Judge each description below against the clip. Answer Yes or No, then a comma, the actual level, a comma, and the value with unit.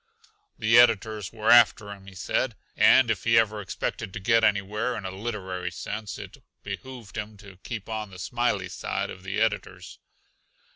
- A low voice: Yes, low, 105 Hz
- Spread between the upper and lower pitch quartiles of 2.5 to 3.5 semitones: Yes, average, 2.9 semitones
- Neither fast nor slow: Yes, average, 180 wpm